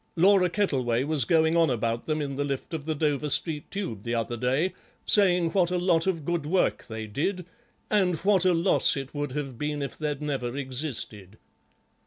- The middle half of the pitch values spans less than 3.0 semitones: No, average, 4.8 semitones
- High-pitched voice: No, medium, 150 Hz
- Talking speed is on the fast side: No, average, 195 wpm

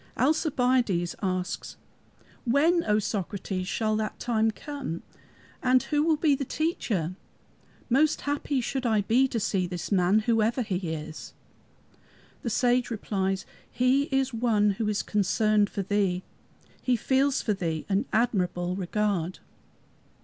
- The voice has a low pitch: No, high, 215 Hz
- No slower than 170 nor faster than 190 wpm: No, slow, 135 wpm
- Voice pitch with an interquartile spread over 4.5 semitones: Yes, average, 5.0 semitones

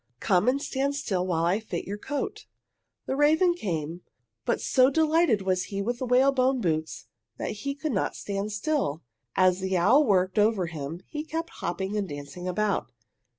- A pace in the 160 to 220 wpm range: Yes, average, 175 wpm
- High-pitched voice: Yes, high, 210 Hz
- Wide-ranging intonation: Yes, wide, 7.2 semitones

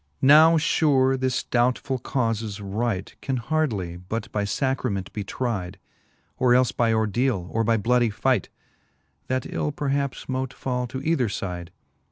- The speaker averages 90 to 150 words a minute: Yes, average, 145 wpm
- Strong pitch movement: No, average, 4.1 semitones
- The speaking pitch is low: Yes, low, 120 Hz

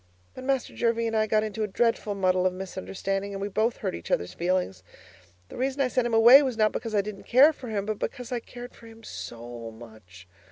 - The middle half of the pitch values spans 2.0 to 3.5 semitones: No, average, 4.3 semitones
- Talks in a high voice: Yes, high, 215 Hz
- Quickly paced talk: Yes, fast, 235 wpm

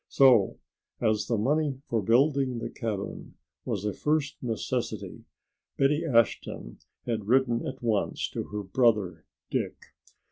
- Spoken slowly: Yes, slow, 130 wpm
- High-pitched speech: No, low, 115 Hz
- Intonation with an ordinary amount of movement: Yes, average, 4.2 semitones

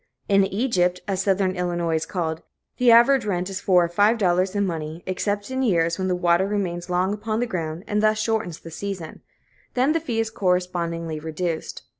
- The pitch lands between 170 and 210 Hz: Yes, medium, 185 Hz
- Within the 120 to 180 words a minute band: No, average, 195 wpm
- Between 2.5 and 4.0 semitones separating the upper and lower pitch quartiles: Yes, average, 3.3 semitones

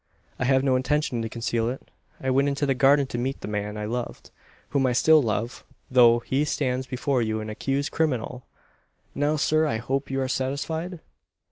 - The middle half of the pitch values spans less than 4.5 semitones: Yes, average, 3.0 semitones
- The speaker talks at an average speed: Yes, average, 195 wpm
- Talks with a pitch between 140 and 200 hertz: No, low, 130 Hz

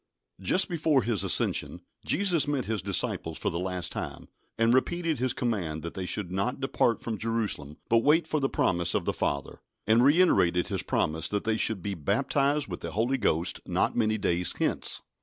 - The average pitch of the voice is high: No, low, 110 Hz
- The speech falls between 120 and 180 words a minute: No, average, 190 wpm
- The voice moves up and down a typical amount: No, wide, 7.0 semitones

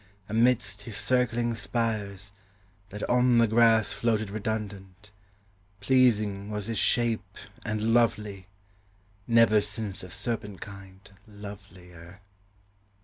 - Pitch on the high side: No, low, 105 Hz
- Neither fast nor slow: No, slow, 100 wpm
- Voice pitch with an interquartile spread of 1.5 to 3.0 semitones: Yes, narrow, 2.6 semitones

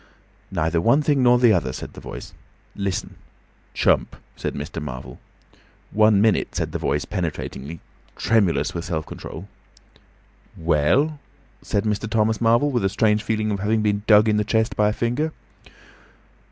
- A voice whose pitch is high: No, low, 105 Hz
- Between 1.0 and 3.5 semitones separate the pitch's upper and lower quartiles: No, average, 4.8 semitones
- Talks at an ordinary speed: Yes, average, 155 wpm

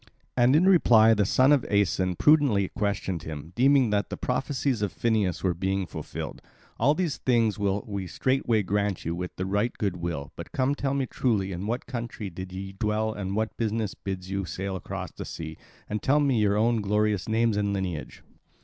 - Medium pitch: No, low, 105 Hz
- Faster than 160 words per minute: Yes, average, 190 wpm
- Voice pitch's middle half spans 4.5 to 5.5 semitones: No, average, 3.9 semitones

